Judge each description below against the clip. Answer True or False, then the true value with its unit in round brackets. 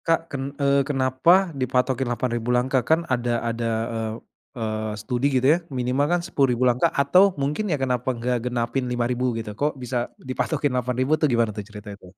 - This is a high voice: False (125 Hz)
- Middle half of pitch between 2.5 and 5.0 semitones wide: True (2.8 semitones)